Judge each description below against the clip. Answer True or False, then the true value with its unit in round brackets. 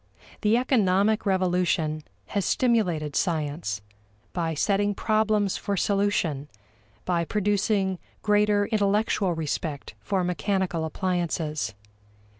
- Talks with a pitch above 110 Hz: True (190 Hz)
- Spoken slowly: True (90 wpm)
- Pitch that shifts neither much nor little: True (4.1 semitones)